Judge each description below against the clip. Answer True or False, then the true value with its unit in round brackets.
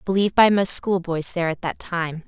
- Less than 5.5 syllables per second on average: False (5.6 syllables/s)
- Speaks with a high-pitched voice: False (180 Hz)